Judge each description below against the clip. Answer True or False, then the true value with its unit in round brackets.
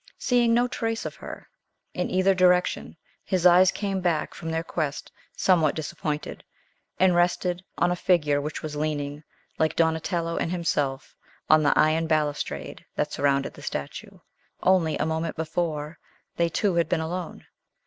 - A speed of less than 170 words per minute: True (155 wpm)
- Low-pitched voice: False (165 Hz)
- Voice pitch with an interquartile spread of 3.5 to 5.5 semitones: False (2.8 semitones)